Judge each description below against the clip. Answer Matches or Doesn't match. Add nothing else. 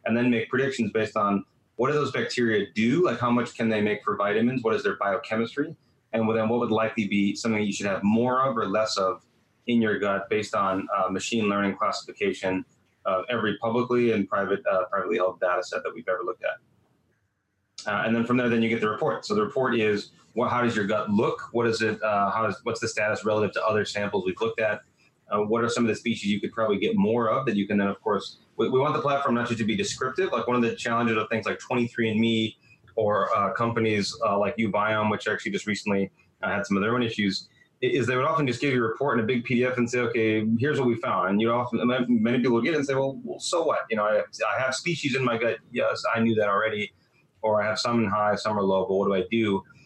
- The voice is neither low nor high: Doesn't match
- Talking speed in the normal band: Doesn't match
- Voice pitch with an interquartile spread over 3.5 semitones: Doesn't match